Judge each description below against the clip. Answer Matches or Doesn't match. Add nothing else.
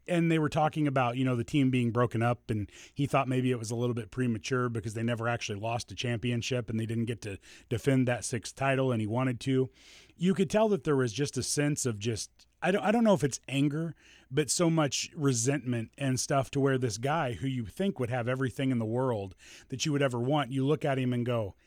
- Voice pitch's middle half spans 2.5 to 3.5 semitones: Matches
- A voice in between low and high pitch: Doesn't match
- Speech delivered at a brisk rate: Matches